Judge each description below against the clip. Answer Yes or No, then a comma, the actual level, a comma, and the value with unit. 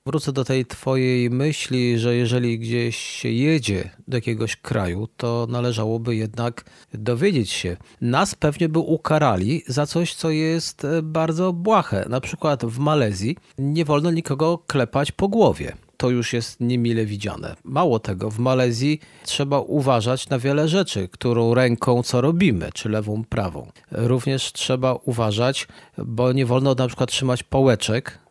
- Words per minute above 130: Yes, average, 145 wpm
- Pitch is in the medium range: No, low, 125 Hz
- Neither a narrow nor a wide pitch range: Yes, average, 4.1 semitones